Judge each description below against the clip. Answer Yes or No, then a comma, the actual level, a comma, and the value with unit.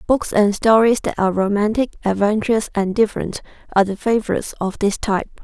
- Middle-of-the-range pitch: No, high, 210 Hz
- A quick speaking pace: No, average, 165 wpm